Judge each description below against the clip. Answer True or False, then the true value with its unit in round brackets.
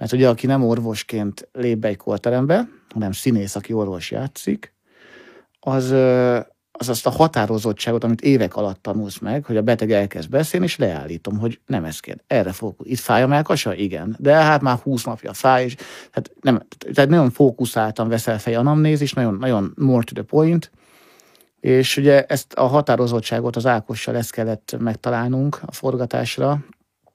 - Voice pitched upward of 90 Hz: True (120 Hz)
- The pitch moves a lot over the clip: False (3.4 semitones)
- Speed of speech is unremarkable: False (165 wpm)